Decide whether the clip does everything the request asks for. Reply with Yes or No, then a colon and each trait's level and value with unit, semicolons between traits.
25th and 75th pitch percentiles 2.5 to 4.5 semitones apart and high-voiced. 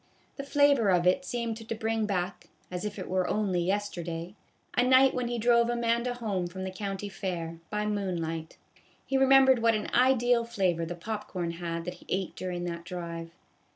No: average, 4.9 semitones; high, 200 Hz